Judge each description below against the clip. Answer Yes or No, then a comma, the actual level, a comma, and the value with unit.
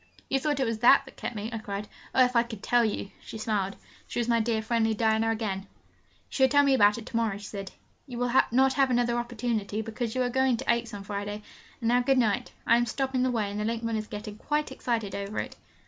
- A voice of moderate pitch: No, high, 230 Hz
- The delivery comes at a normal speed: No, fast, 255 wpm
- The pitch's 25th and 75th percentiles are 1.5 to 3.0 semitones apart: Yes, narrow, 2.6 semitones